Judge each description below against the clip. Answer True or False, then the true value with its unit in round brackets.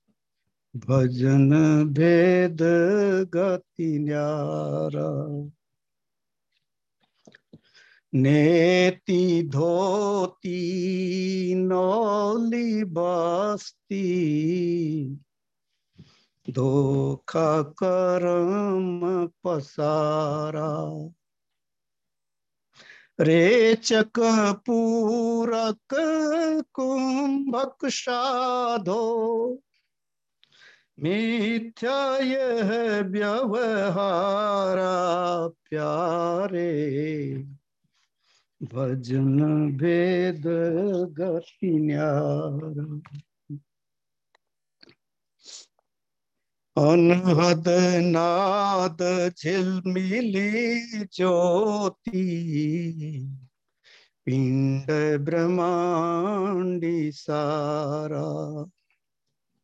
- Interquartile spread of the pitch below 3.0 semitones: False (4.9 semitones)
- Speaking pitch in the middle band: True (175 Hz)